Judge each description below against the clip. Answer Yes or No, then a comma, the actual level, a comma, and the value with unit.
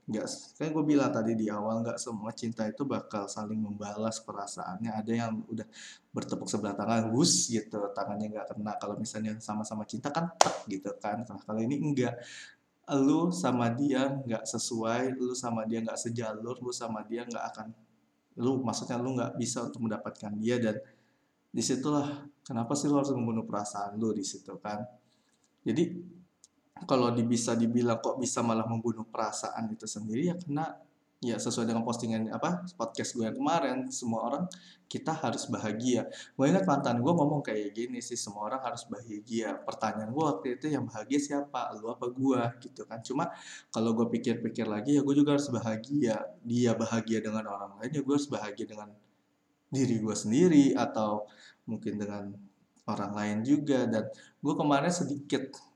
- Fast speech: Yes, fast, 165 wpm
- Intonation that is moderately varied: Yes, average, 3.4 semitones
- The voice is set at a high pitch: No, low, 115 Hz